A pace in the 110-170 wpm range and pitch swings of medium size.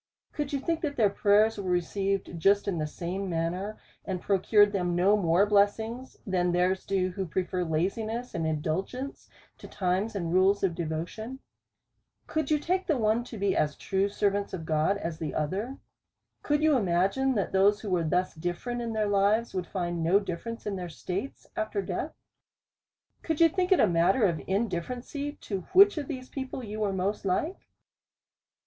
No: average, 180 wpm; average, 4.4 semitones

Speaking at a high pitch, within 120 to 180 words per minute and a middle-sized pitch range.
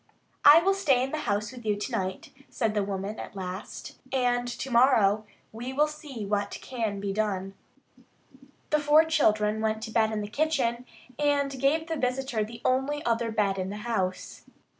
Yes: high, 235 Hz; average, 175 wpm; average, 4.5 semitones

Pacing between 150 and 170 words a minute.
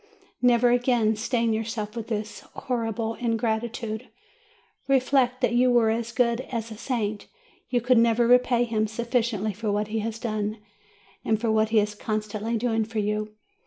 Yes: average, 160 wpm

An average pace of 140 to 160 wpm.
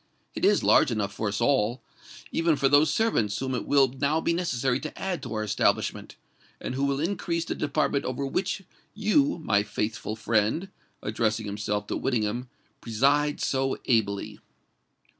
Yes: average, 150 wpm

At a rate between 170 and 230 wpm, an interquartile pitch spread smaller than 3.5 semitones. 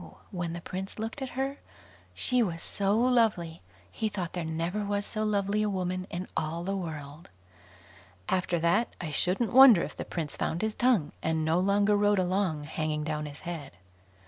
No: average, 180 wpm; average, 4.4 semitones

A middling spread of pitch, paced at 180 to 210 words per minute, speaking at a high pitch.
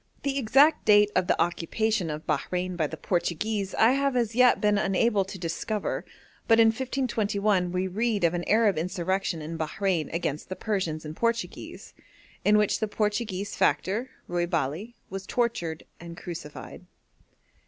No: average, 4.3 semitones; average, 155 wpm; high, 195 Hz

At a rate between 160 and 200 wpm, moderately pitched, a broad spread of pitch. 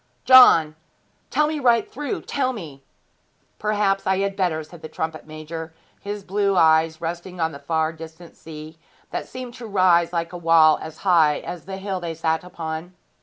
No: average, 175 wpm; medium, 170 Hz; average, 3.7 semitones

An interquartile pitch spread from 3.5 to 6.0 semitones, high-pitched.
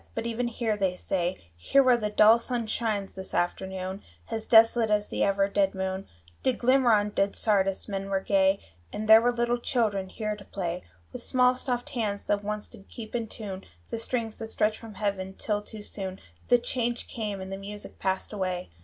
No: average, 3.0 semitones; high, 210 Hz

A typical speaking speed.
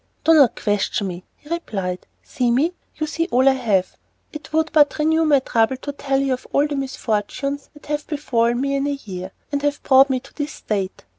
No: fast, 210 wpm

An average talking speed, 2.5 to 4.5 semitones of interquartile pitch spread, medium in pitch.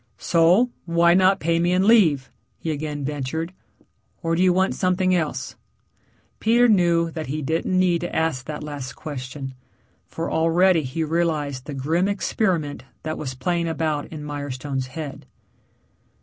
Yes: average, 150 wpm; average, 3.4 semitones; medium, 160 Hz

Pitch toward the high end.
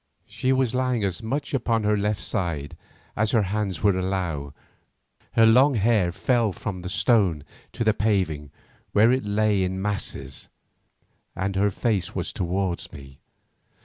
No: low, 100 Hz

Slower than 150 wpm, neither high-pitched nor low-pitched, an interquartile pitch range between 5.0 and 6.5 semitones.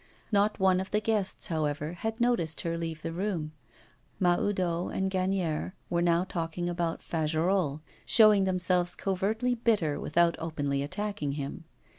No: average, 140 wpm; medium, 175 Hz; average, 3.3 semitones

